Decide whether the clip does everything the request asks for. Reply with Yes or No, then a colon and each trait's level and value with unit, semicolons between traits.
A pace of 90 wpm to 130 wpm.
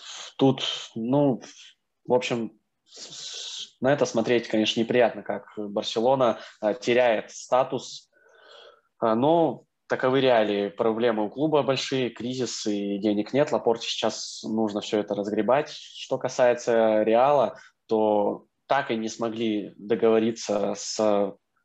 Yes: slow, 110 wpm